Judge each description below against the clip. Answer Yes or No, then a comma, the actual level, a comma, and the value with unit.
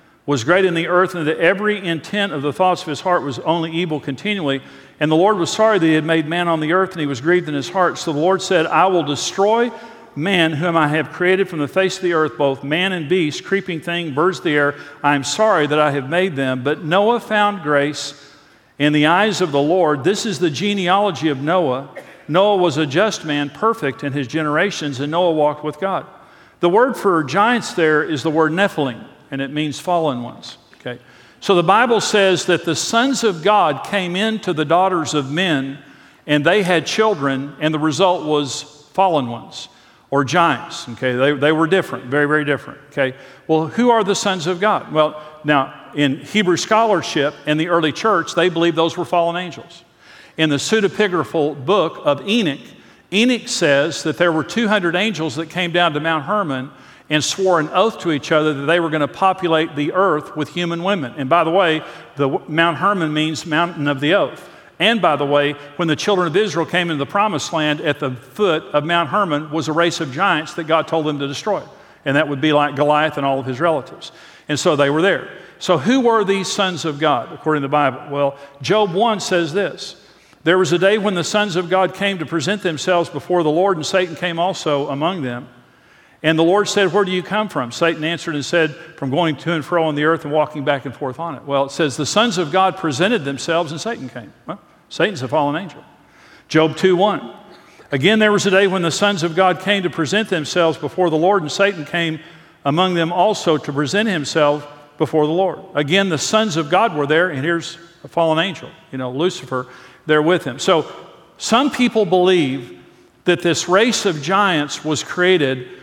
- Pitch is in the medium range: Yes, medium, 165 Hz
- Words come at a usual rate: No, fast, 215 wpm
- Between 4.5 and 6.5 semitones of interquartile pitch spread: No, average, 3.9 semitones